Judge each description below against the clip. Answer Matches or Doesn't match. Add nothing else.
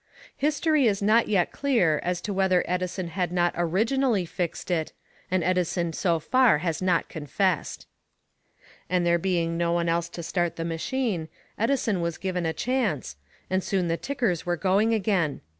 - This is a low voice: Doesn't match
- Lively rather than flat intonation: Doesn't match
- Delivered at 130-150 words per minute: Doesn't match